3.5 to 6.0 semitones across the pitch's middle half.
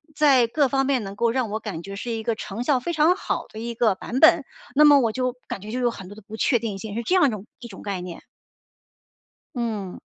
Yes: average, 3.9 semitones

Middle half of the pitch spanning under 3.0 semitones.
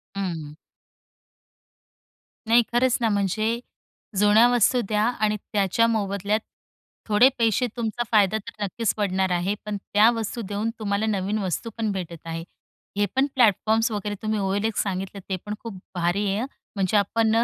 Yes: narrow, 2.4 semitones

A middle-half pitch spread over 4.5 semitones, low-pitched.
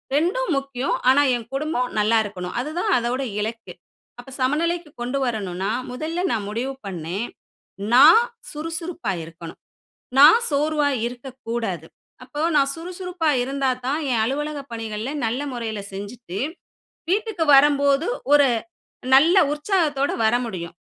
No: average, 5.2 semitones; very high, 270 Hz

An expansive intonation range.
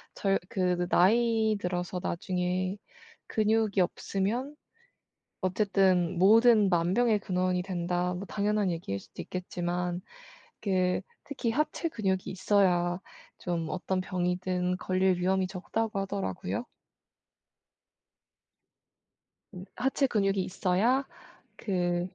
No: average, 2.7 semitones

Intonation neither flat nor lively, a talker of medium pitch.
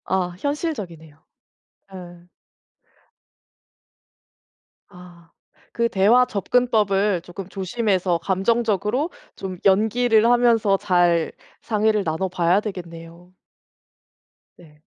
No: average, 4.0 semitones; high, 195 Hz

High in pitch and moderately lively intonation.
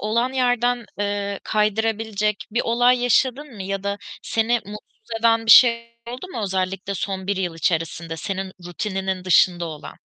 Yes: high, 210 Hz; average, 3.5 semitones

